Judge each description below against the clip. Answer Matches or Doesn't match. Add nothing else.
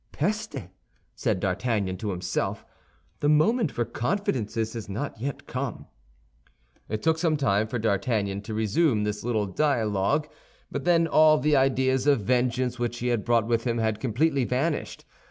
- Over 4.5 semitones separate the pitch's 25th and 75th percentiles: Matches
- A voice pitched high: Doesn't match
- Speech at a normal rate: Matches